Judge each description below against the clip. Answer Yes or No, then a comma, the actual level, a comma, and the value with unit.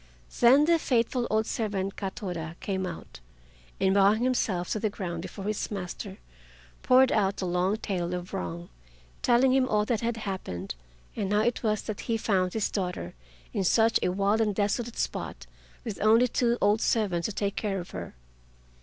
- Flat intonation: No, average, 3.5 semitones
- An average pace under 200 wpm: Yes, average, 180 wpm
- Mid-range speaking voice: No, high, 205 Hz